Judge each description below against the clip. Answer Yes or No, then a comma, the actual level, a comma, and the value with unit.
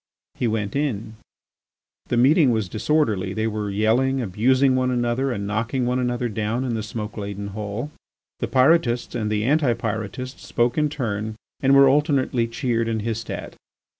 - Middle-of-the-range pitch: No, low, 120 Hz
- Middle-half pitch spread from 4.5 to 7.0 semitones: No, average, 3.4 semitones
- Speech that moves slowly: No, average, 165 wpm